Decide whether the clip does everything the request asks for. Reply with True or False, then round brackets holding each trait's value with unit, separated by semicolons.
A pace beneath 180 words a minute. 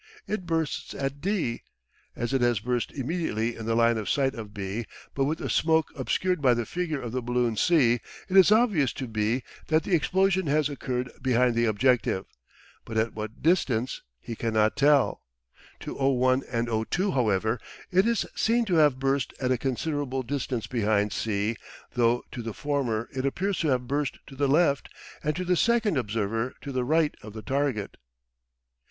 False (185 wpm)